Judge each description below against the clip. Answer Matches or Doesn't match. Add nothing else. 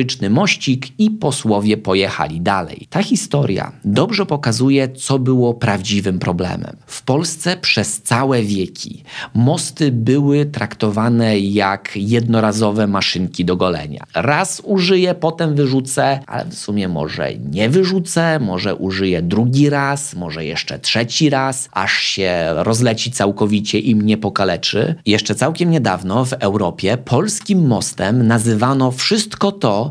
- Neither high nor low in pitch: Doesn't match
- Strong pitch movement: Matches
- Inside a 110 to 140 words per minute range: Matches